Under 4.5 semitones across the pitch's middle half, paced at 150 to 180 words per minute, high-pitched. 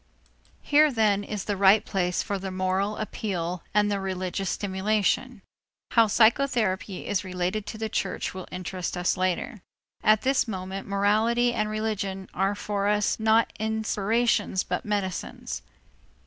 No: narrow, 2.5 semitones; average, 140 wpm; high, 205 Hz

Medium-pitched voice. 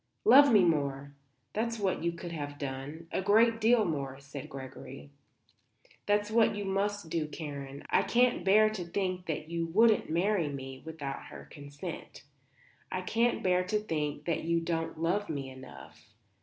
Yes: medium, 170 Hz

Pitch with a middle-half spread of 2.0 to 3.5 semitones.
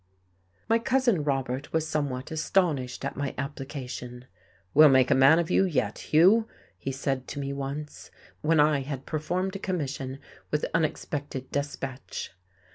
Yes: average, 3.0 semitones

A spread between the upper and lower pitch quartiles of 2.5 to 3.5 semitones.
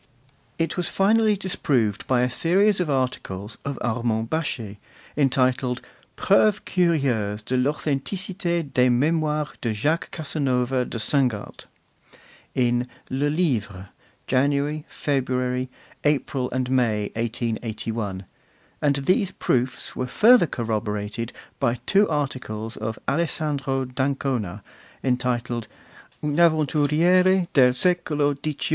No: average, 4.4 semitones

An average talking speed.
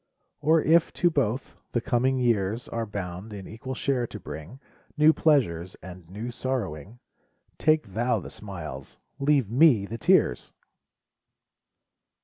No: slow, 130 wpm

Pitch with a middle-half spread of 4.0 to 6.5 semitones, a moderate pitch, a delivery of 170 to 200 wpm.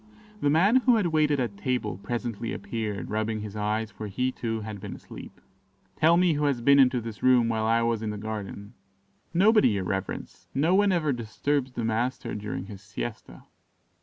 No: average, 5.1 semitones; low, 115 Hz; average, 190 wpm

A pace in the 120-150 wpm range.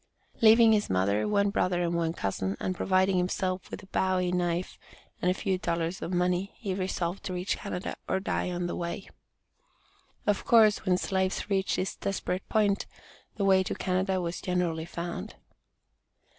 No: average, 170 wpm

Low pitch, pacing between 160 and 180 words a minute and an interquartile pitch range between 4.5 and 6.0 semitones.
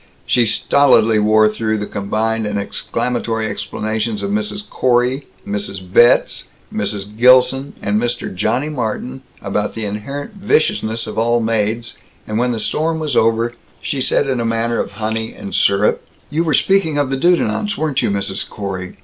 No: low, 115 Hz; average, 165 wpm; average, 3.5 semitones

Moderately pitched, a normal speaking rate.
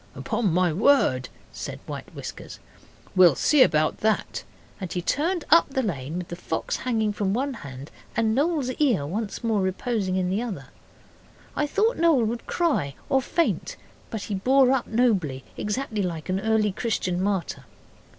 No: high, 215 Hz; average, 165 wpm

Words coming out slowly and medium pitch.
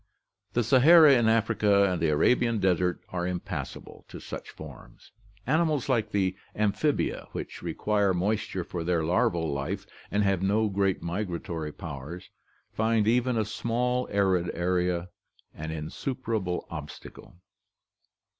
No: slow, 125 wpm; low, 100 Hz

